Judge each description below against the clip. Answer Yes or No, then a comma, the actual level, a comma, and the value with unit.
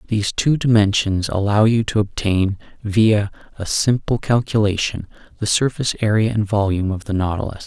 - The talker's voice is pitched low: Yes, low, 105 Hz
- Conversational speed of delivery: Yes, average, 150 wpm